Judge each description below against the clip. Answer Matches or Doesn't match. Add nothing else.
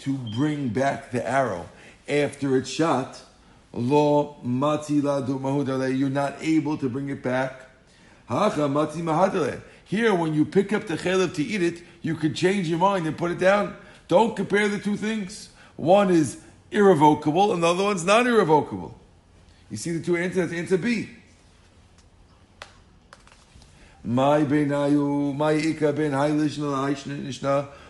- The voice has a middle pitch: Matches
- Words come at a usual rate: Doesn't match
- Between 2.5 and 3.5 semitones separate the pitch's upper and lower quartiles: Doesn't match